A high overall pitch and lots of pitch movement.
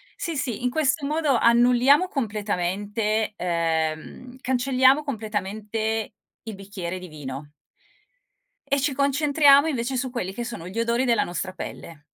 Yes: high, 230 Hz; wide, 5.7 semitones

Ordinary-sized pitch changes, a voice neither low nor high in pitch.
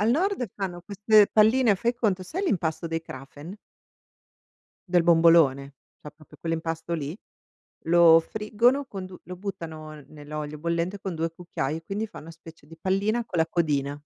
Yes: average, 4.3 semitones; medium, 170 Hz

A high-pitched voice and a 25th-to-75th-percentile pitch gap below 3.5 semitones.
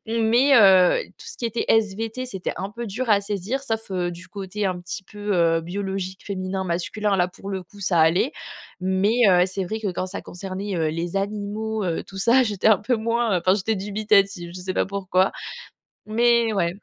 Yes: high, 200 Hz; average, 3.1 semitones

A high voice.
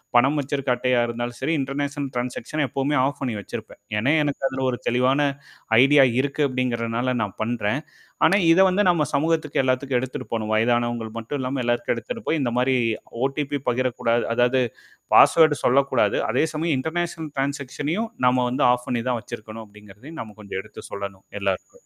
No: low, 130 Hz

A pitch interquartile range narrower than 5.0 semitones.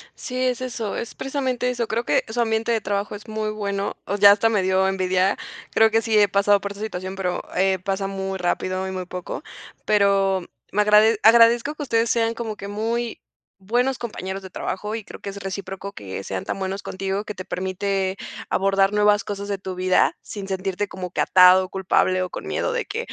Yes: average, 2.8 semitones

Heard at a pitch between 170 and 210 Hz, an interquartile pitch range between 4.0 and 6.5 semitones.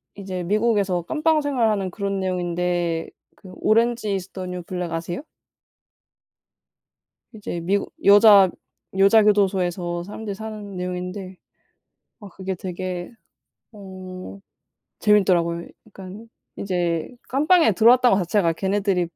No: high, 190 Hz; average, 2.8 semitones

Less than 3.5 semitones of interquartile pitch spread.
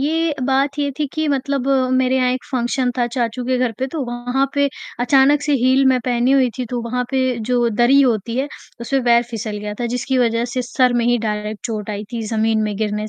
Yes: narrow, 2.4 semitones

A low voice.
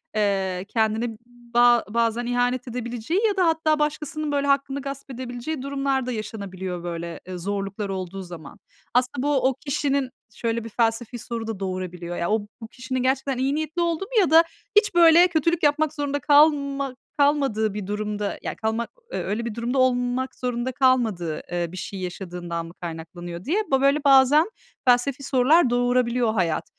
No: high, 245 Hz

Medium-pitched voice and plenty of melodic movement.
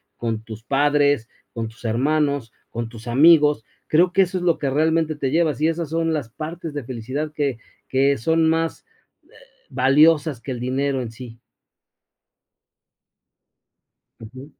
No: medium, 145 Hz; average, 4.6 semitones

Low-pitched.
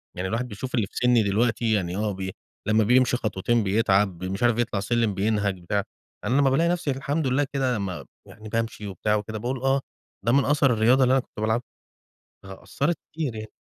Yes: low, 115 Hz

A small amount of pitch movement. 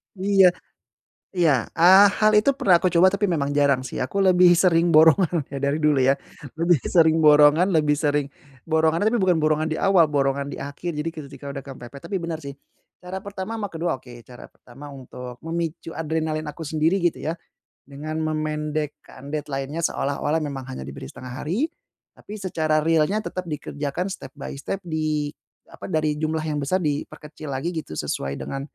No: average, 3.3 semitones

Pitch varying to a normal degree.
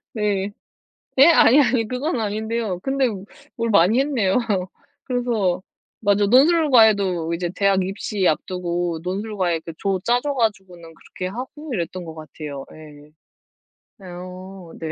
Yes: average, 5.0 semitones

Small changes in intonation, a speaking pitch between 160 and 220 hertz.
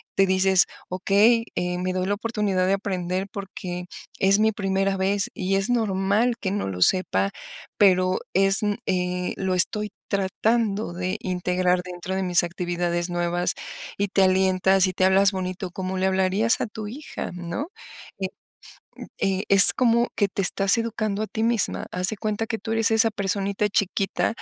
Yes: narrow, 2.1 semitones; high, 190 Hz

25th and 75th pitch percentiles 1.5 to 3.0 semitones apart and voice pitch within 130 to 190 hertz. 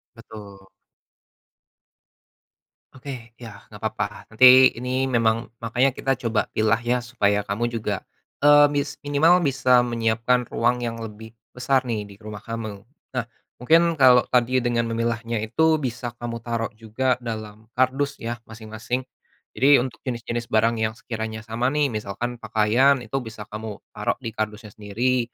No: narrow, 2.5 semitones; low, 115 Hz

